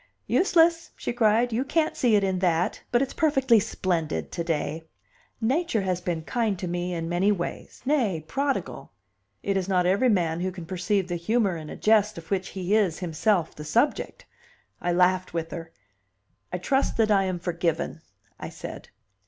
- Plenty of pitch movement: No, average, 4.6 semitones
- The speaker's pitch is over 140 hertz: Yes, medium, 185 Hz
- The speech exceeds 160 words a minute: Yes, average, 180 wpm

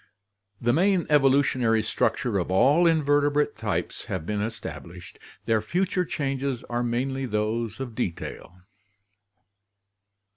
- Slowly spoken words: Yes, slow, 110 wpm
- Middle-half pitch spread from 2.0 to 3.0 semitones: No, average, 4.8 semitones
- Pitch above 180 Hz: No, low, 120 Hz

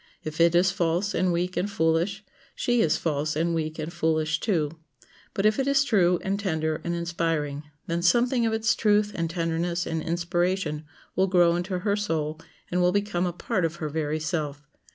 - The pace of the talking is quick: No, average, 195 wpm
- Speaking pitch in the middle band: Yes, medium, 170 Hz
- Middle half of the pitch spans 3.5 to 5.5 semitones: No, average, 3.1 semitones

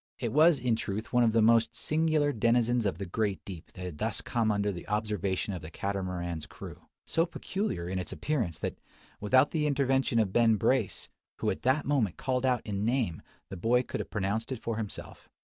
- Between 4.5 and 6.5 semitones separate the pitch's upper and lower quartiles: Yes, average, 4.9 semitones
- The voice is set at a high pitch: No, low, 110 Hz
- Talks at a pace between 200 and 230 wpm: Yes, fast, 205 wpm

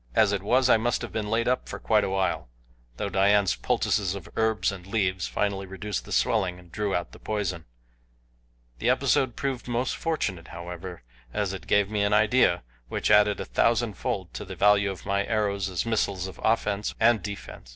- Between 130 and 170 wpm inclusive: No, average, 195 wpm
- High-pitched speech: No, low, 100 Hz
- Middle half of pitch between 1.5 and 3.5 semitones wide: Yes, narrow, 2.6 semitones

